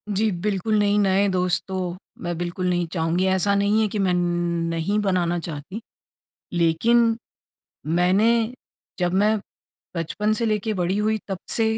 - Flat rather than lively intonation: No, average, 3.2 semitones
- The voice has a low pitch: No, high, 190 Hz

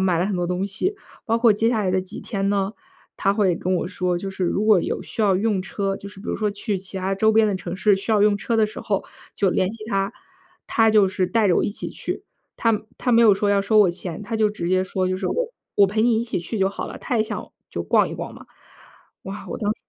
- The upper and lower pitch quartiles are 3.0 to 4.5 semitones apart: No, narrow, 2.5 semitones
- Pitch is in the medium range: No, high, 200 Hz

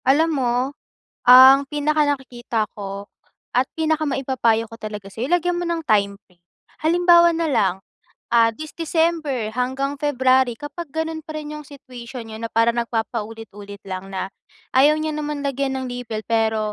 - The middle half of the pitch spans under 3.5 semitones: No, average, 5.2 semitones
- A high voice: Yes, very high, 260 Hz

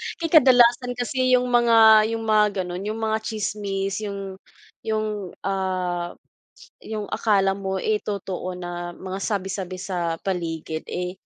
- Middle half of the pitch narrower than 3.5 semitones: Yes, average, 3.0 semitones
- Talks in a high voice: Yes, high, 195 Hz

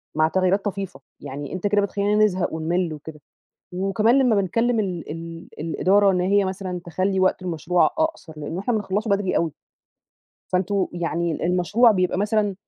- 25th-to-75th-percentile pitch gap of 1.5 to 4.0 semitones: Yes, average, 3.1 semitones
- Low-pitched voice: No, medium, 185 Hz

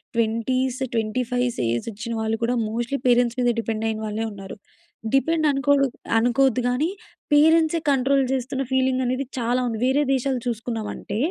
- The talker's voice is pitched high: Yes, very high, 250 Hz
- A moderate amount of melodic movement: Yes, average, 3.1 semitones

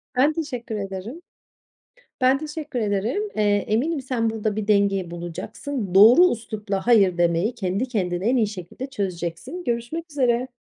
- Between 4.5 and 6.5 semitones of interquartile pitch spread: Yes, average, 4.9 semitones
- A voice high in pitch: Yes, high, 220 Hz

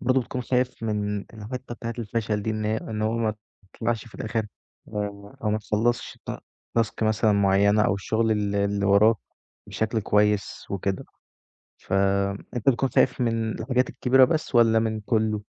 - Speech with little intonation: Yes, narrow, 2.1 semitones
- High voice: No, low, 110 Hz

